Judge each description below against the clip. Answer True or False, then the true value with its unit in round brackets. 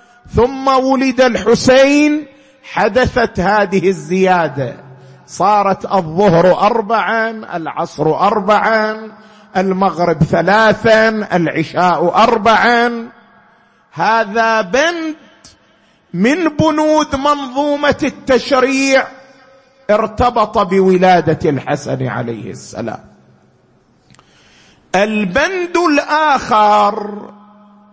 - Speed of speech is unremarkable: False (60 wpm)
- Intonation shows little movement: False (5.1 semitones)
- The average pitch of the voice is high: True (220 Hz)